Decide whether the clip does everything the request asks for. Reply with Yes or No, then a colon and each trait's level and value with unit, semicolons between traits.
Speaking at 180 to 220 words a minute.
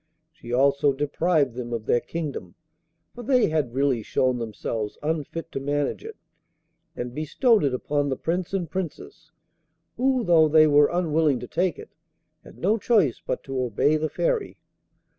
No: average, 160 wpm